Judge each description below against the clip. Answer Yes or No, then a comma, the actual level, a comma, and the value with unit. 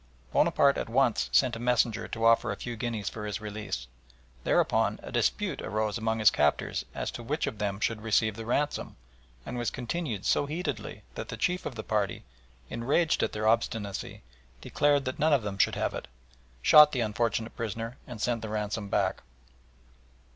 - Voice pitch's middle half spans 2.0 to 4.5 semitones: Yes, average, 3.2 semitones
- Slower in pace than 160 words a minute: No, average, 185 wpm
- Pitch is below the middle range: Yes, low, 115 Hz